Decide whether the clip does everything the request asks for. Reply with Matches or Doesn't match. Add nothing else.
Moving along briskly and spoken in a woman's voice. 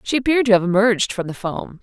Matches